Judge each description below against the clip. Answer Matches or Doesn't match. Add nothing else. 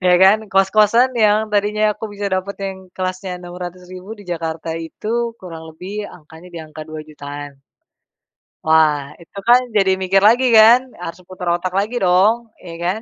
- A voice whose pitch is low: Doesn't match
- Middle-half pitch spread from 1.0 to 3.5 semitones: Doesn't match